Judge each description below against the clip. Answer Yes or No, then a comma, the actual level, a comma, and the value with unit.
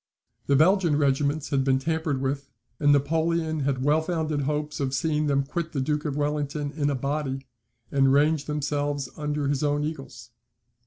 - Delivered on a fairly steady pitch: Yes, narrow, 1.7 semitones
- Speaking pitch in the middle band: Yes, medium, 145 Hz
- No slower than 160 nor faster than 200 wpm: Yes, average, 170 wpm